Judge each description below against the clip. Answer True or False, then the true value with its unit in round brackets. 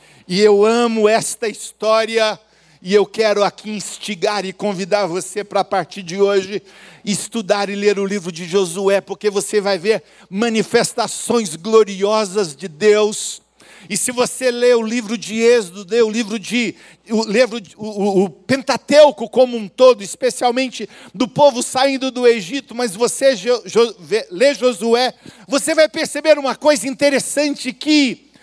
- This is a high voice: True (220 Hz)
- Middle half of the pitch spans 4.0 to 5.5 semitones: False (3.6 semitones)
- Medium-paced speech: True (150 wpm)